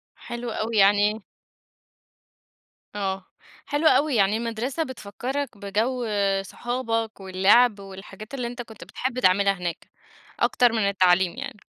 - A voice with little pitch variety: No, average, 3.7 semitones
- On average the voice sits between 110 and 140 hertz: No, high, 220 Hz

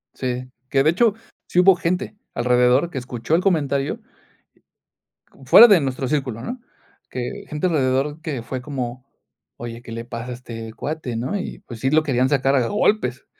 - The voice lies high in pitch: No, low, 130 Hz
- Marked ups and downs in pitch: No, average, 4.2 semitones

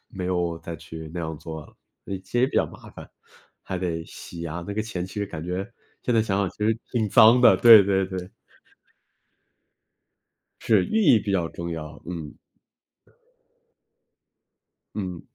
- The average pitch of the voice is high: No, very low, 90 Hz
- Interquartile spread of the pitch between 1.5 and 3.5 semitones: No, average, 4.0 semitones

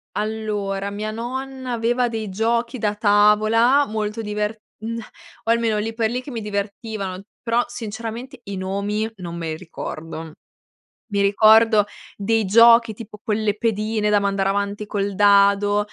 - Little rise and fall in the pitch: Yes, narrow, 2.2 semitones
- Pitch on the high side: Yes, high, 215 Hz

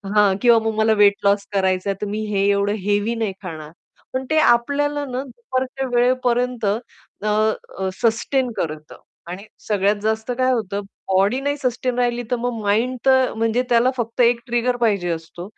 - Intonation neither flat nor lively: Yes, average, 3.7 semitones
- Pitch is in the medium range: No, high, 230 Hz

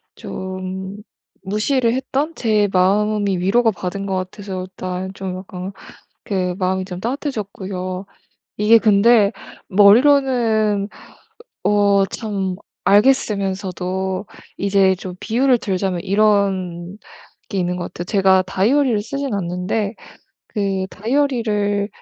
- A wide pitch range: No, narrow, 2.6 semitones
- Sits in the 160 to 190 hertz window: No, high, 200 Hz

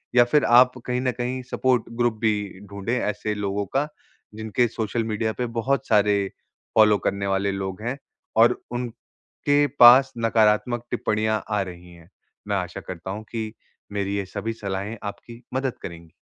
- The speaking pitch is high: No, low, 110 Hz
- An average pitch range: Yes, average, 3.4 semitones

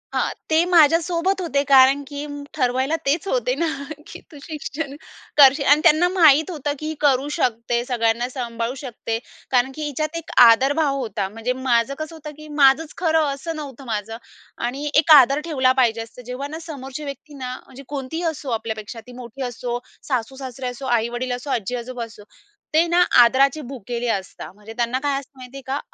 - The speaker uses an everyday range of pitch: Yes, average, 3.8 semitones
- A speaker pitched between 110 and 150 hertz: No, very high, 270 Hz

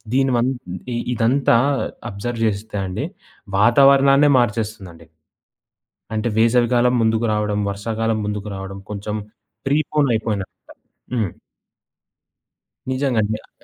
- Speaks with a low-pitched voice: Yes, low, 115 Hz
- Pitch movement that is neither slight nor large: Yes, average, 3.0 semitones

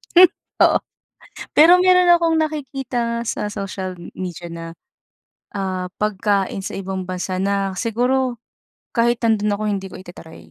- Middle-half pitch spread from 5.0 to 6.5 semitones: Yes, wide, 5.4 semitones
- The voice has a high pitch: Yes, high, 210 Hz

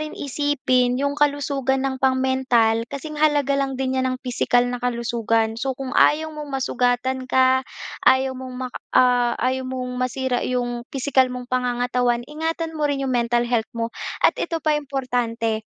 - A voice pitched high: Yes, very high, 260 Hz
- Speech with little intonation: Yes, narrow, 1.9 semitones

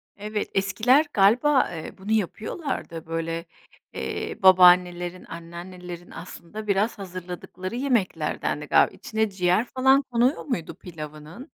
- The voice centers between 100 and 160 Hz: No, high, 190 Hz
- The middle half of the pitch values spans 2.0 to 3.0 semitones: No, average, 4.1 semitones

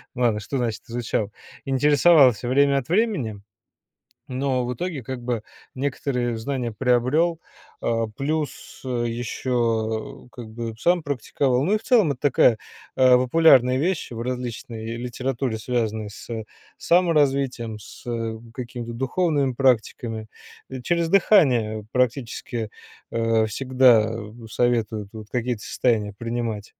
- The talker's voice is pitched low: Yes, low, 125 Hz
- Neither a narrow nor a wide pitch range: Yes, average, 3.2 semitones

